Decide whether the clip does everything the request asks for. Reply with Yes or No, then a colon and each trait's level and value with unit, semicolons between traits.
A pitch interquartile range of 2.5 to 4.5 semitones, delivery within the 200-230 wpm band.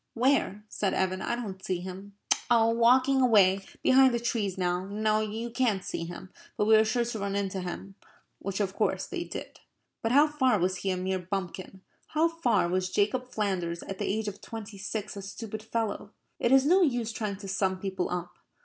Yes: average, 3.7 semitones; fast, 205 wpm